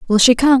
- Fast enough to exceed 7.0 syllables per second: No, 6.5 syllables/s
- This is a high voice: Yes, high, 245 Hz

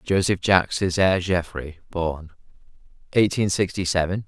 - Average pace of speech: No, slow, 110 wpm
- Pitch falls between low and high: No, very low, 90 Hz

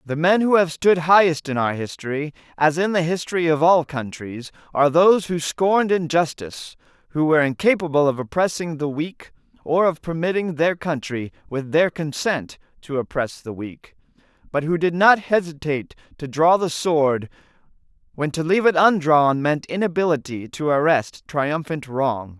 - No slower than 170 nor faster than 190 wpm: No, average, 160 wpm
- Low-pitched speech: No, medium, 155 Hz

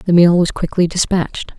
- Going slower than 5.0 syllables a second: No, 5.3 syllables/s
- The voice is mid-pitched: Yes, medium, 175 Hz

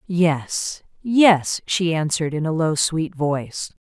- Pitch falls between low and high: Yes, medium, 165 Hz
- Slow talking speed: Yes, slow, 125 wpm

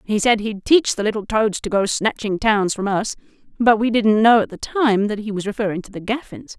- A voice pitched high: Yes, high, 215 Hz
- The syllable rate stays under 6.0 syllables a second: Yes, 5.3 syllables/s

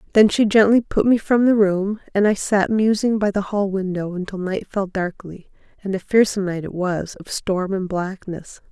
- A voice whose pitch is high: Yes, high, 195 Hz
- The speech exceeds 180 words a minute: Yes, average, 200 wpm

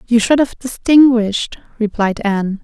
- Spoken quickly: No, slow, 135 wpm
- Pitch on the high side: Yes, high, 230 Hz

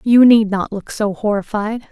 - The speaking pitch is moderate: No, high, 215 Hz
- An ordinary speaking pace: Yes, average, 190 wpm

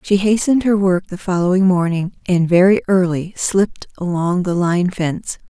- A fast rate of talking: No, average, 165 wpm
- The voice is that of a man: No, female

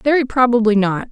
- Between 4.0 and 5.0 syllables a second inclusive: No, 5.7 syllables/s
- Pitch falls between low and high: No, high, 235 Hz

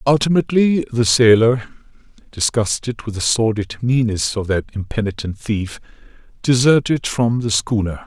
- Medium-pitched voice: No, low, 115 Hz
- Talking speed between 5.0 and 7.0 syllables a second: No, 4.7 syllables/s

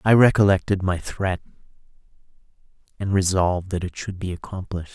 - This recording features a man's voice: Yes, male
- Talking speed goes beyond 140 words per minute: No, slow, 135 wpm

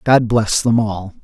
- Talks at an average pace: Yes, average, 195 wpm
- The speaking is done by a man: Yes, male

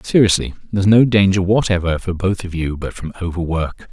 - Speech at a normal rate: Yes, average, 185 wpm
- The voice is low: Yes, very low, 95 Hz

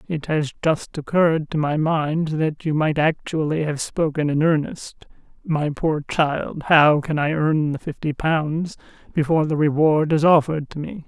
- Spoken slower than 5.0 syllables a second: Yes, 4.4 syllables/s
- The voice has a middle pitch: Yes, medium, 155 Hz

